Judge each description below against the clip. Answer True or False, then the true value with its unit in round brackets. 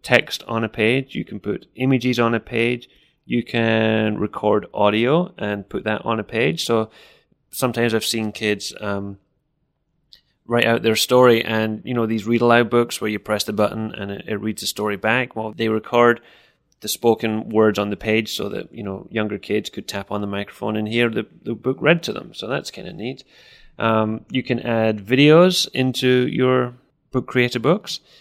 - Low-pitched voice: True (115 Hz)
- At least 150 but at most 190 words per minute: False (200 wpm)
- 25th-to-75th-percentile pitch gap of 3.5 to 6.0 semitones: False (2.8 semitones)